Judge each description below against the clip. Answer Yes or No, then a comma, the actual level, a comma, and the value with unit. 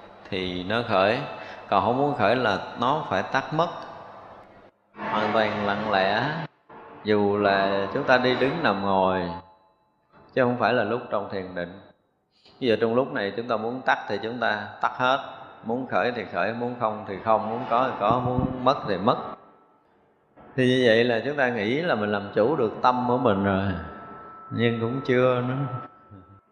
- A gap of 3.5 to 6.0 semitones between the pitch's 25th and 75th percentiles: Yes, average, 4.2 semitones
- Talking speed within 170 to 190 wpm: Yes, average, 185 wpm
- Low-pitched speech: Yes, low, 110 Hz